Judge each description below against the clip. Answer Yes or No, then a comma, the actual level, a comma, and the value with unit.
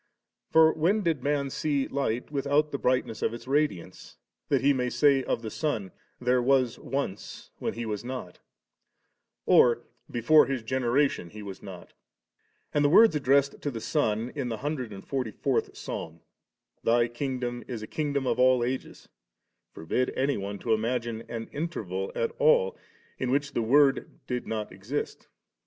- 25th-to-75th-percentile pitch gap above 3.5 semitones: Yes, average, 3.9 semitones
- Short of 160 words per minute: No, average, 175 wpm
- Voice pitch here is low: Yes, low, 125 Hz